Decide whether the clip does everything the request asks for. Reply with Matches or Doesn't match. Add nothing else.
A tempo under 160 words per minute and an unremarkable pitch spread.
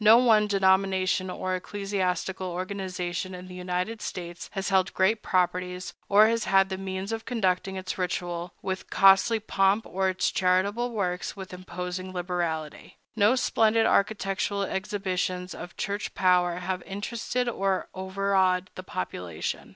Doesn't match